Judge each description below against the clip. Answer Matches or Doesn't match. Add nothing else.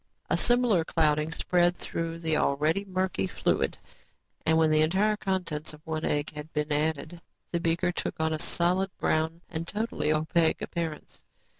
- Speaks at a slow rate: Doesn't match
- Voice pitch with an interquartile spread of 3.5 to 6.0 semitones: Doesn't match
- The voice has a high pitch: Doesn't match